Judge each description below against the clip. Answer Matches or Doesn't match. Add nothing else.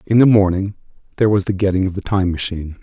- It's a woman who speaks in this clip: Doesn't match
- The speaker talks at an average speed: Doesn't match